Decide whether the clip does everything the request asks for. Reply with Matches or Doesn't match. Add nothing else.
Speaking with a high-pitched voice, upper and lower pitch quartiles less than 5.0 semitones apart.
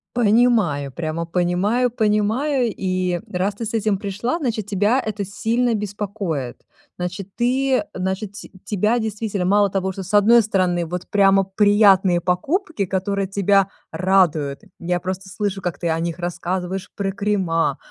Matches